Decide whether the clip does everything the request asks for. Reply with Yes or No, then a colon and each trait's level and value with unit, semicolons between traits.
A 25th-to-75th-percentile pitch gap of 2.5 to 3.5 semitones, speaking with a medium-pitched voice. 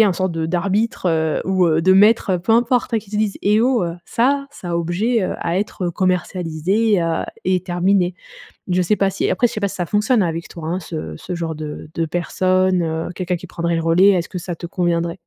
Yes: average, 3.0 semitones; medium, 180 Hz